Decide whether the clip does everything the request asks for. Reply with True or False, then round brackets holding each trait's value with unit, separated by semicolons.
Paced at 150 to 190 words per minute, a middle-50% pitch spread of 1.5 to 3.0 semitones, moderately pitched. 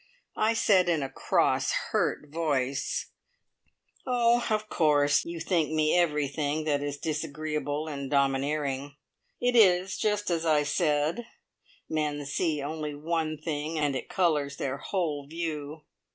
False (135 wpm; 2.7 semitones; 155 Hz)